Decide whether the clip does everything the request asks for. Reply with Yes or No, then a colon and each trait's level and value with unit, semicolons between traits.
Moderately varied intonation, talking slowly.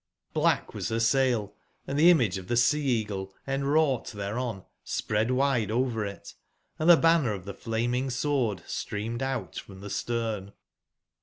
No: average, 4.5 semitones; average, 155 wpm